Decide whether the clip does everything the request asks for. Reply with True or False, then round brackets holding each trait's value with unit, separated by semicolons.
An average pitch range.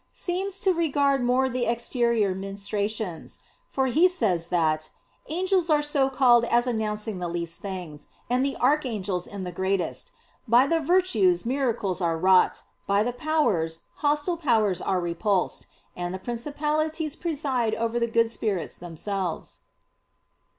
False (7.5 semitones)